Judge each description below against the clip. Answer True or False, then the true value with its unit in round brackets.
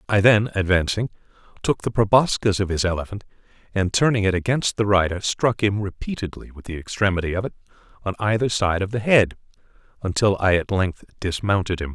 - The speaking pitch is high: False (100 Hz)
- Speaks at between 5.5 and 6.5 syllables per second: True (5.8 syllables/s)